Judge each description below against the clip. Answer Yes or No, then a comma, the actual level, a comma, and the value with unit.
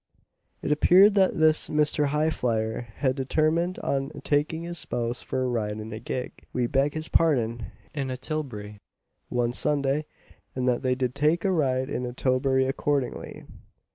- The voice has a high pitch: No, low, 135 Hz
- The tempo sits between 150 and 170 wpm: Yes, average, 165 wpm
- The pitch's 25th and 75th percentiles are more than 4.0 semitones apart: No, average, 3.7 semitones